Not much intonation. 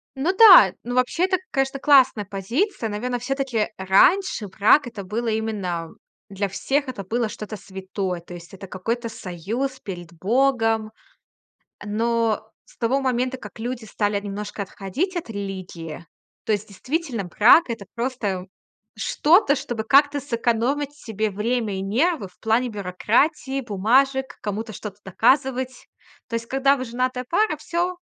No: average, 4.8 semitones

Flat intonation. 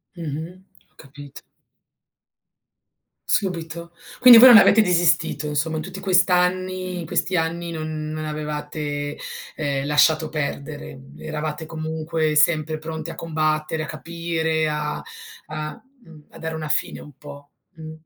Yes: narrow, 1.9 semitones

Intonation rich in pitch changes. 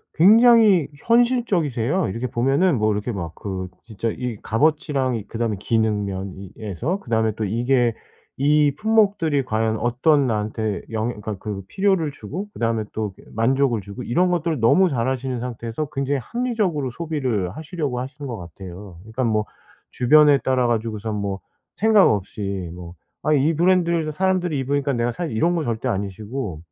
Yes: wide, 6.2 semitones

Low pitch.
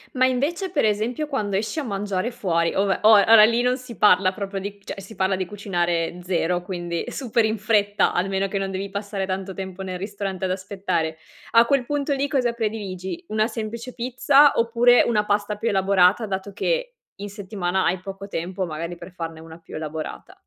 No: high, 200 Hz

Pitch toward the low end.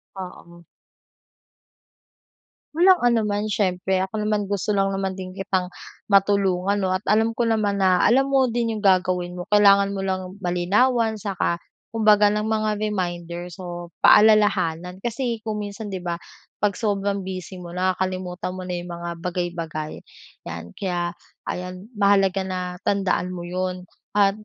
No: high, 190 Hz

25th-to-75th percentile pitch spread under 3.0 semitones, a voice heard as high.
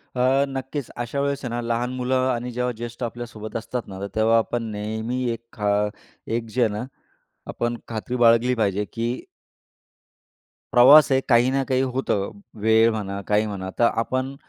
No: narrow, 2.4 semitones; low, 120 Hz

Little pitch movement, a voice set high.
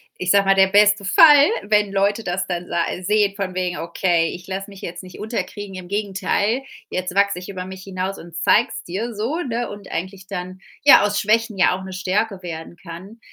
Yes: narrow, 2.1 semitones; high, 195 Hz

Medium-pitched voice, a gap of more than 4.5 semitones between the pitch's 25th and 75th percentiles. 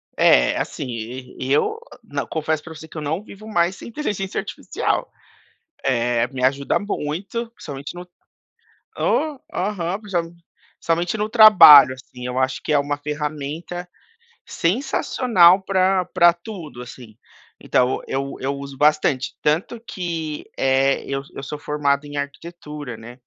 Yes: medium, 150 Hz; average, 4.9 semitones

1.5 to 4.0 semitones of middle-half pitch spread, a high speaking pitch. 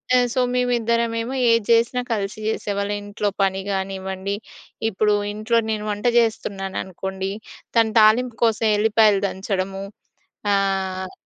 Yes: average, 2.9 semitones; high, 205 Hz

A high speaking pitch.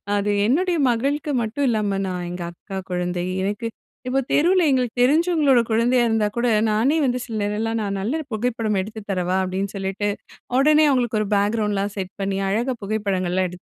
Yes: high, 220 Hz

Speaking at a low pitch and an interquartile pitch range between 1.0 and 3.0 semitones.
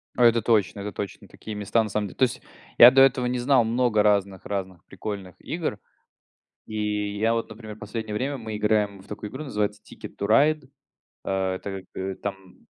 Yes: low, 105 Hz; narrow, 2.6 semitones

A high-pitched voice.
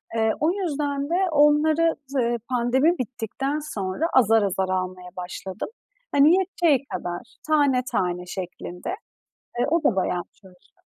Yes: very high, 255 Hz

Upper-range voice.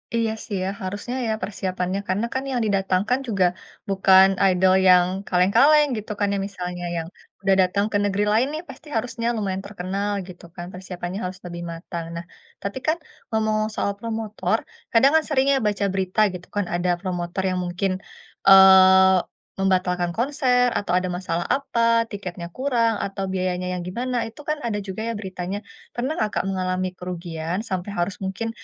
Yes: high, 195 Hz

